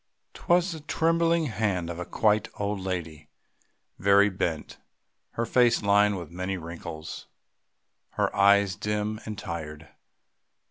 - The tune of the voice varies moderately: Yes, average, 3.9 semitones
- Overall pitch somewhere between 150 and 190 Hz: No, low, 100 Hz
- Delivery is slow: Yes, slow, 125 wpm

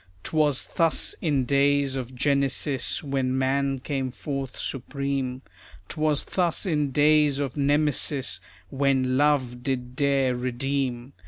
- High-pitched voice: No, medium, 140 Hz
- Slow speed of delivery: Yes, slow, 115 wpm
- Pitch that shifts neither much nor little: No, narrow, 1.9 semitones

